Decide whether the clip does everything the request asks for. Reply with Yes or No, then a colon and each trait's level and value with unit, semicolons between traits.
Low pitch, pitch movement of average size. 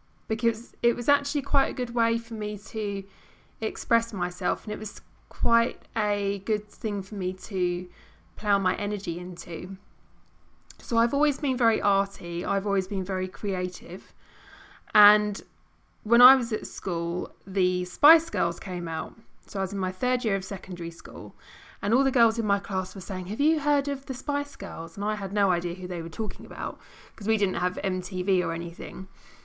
No: high, 200 Hz; average, 3.8 semitones